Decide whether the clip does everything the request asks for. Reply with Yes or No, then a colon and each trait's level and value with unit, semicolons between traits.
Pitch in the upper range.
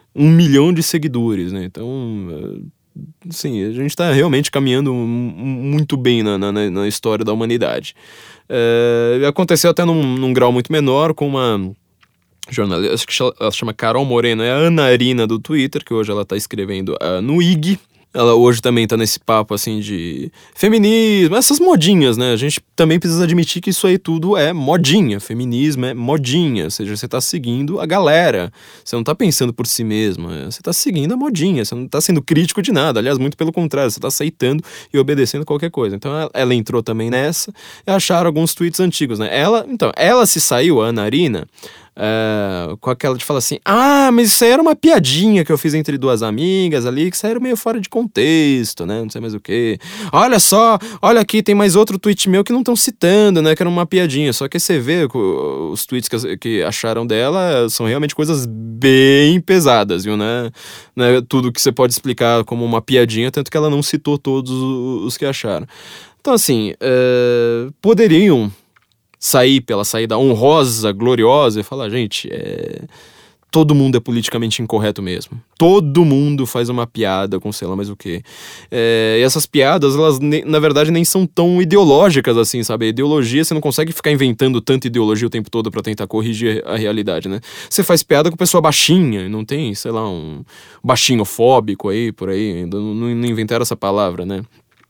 No: low, 135 Hz